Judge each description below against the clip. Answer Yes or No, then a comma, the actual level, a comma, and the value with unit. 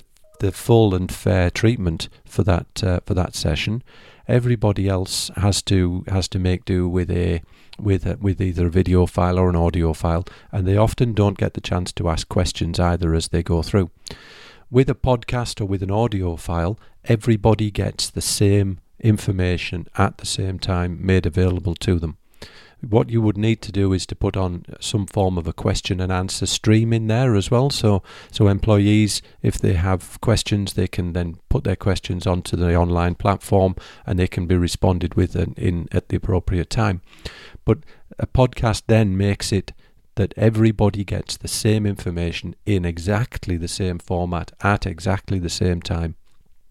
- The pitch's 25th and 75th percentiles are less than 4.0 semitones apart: Yes, average, 3.2 semitones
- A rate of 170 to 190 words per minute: Yes, average, 180 wpm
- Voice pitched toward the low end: Yes, very low, 95 Hz